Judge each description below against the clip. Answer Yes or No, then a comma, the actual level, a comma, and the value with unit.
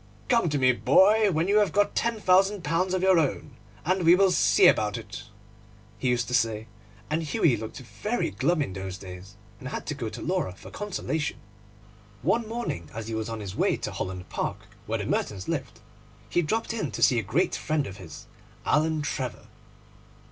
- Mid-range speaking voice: Yes, medium, 150 Hz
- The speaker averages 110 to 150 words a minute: No, average, 200 wpm